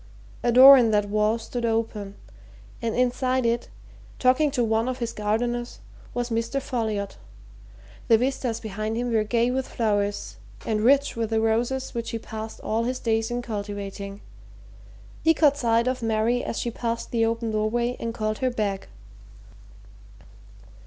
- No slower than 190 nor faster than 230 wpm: No, average, 160 wpm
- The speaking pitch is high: Yes, high, 230 Hz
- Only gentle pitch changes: Yes, narrow, 2.1 semitones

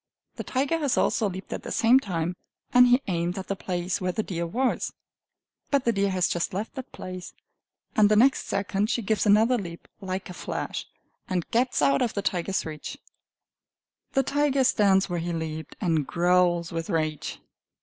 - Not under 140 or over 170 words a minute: No, average, 185 wpm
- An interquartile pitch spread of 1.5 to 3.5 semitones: No, average, 5.1 semitones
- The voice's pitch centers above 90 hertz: Yes, high, 190 Hz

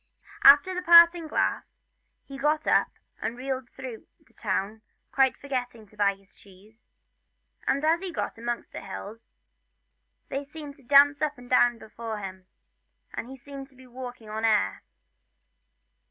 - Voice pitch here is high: Yes, very high, 255 Hz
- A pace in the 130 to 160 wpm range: Yes, average, 155 wpm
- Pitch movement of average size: Yes, average, 4.4 semitones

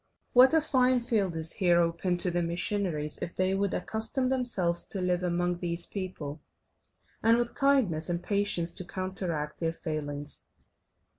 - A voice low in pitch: No, medium, 180 Hz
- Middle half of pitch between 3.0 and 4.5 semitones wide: Yes, average, 3.8 semitones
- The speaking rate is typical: Yes, average, 155 wpm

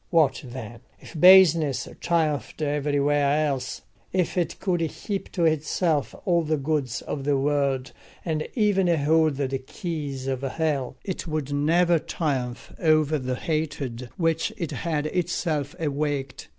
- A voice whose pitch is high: No, medium, 150 Hz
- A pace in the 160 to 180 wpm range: No, slow, 135 wpm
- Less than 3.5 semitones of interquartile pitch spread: Yes, average, 3.1 semitones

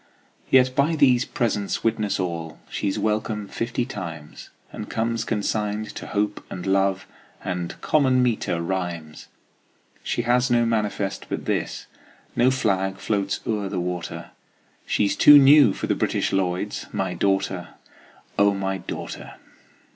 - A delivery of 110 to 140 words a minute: Yes, slow, 135 wpm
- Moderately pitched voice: No, low, 105 Hz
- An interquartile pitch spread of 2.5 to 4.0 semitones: Yes, average, 3.7 semitones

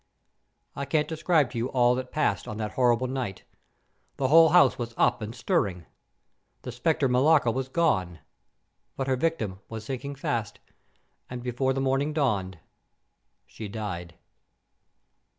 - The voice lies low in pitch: Yes, low, 125 Hz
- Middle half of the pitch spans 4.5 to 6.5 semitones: No, average, 4.1 semitones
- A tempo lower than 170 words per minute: Yes, average, 145 wpm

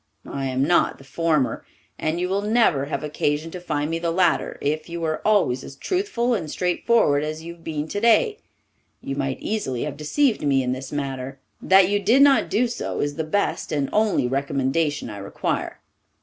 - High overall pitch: No, medium, 155 Hz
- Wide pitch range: Yes, wide, 6.3 semitones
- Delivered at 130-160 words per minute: No, average, 190 wpm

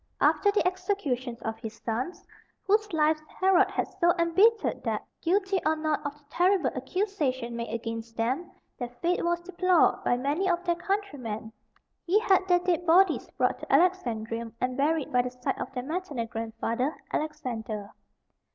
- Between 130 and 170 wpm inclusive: Yes, average, 160 wpm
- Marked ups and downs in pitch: Yes, wide, 7.0 semitones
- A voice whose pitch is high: Yes, very high, 310 Hz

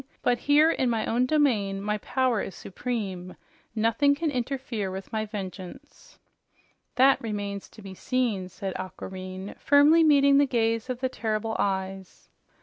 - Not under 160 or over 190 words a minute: No, average, 145 wpm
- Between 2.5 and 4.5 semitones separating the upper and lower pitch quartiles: No, average, 5.1 semitones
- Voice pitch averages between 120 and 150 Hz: No, high, 225 Hz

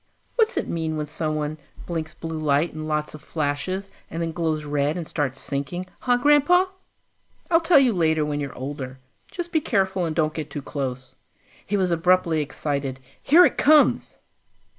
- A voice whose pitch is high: No, medium, 160 Hz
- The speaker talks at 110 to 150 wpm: No, average, 175 wpm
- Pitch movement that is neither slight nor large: Yes, average, 4.5 semitones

